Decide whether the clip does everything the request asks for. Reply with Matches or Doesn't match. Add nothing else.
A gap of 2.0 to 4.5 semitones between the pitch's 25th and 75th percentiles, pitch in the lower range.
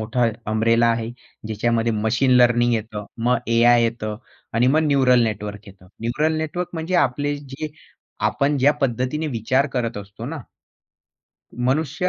Matches